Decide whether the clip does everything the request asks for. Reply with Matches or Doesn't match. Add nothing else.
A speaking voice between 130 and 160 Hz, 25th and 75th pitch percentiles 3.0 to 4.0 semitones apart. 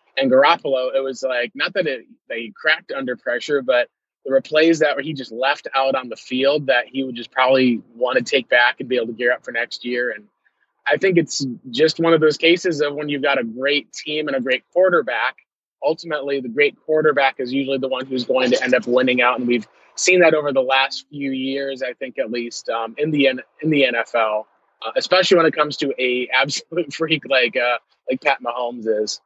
Matches